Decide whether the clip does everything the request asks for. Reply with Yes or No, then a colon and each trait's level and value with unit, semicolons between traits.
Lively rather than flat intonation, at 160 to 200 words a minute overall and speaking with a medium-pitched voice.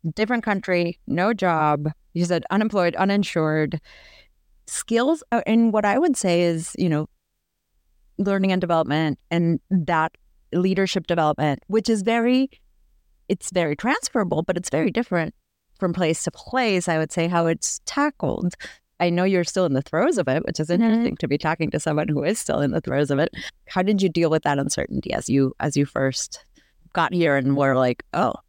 No: average, 4.3 semitones; average, 185 wpm; medium, 175 Hz